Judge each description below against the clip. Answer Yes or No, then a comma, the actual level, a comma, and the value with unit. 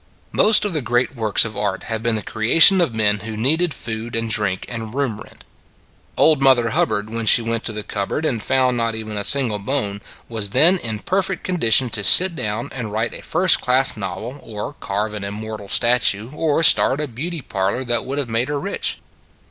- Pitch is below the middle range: Yes, low, 115 Hz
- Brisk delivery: Yes, fast, 210 wpm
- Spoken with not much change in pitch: No, average, 4.5 semitones